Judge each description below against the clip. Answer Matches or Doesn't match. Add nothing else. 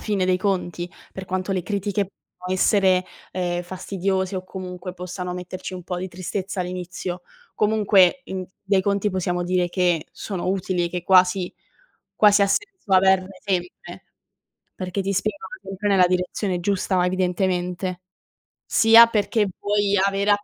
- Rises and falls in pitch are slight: Matches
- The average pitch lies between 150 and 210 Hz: Matches